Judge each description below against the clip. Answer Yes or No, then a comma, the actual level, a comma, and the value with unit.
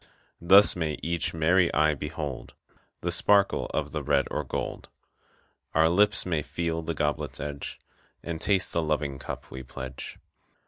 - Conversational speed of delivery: Yes, average, 150 wpm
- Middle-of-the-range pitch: No, very low, 80 Hz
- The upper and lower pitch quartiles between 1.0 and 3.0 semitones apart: Yes, average, 2.7 semitones